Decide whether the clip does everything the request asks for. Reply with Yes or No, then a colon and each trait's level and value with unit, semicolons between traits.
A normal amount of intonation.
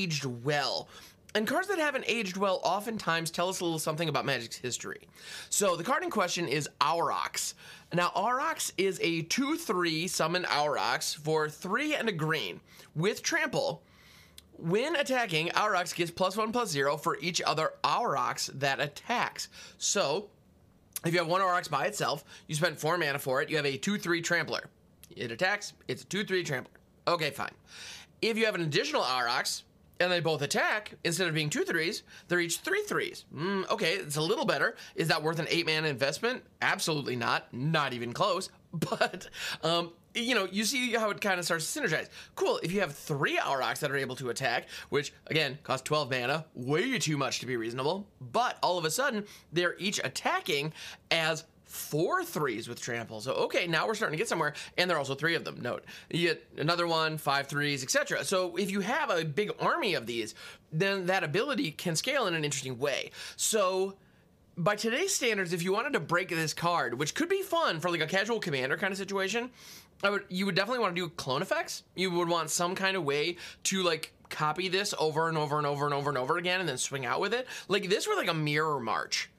Yes: average, 4.8 semitones